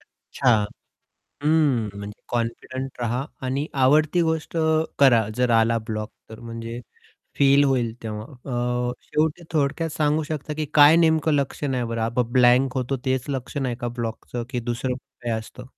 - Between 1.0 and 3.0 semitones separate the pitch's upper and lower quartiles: No, average, 3.9 semitones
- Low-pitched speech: Yes, low, 130 Hz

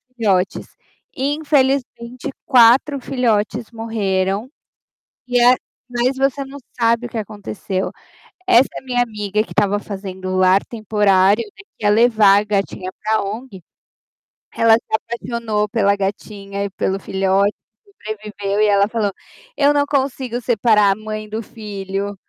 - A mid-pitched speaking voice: No, high, 215 Hz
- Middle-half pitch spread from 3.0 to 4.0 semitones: Yes, average, 3.4 semitones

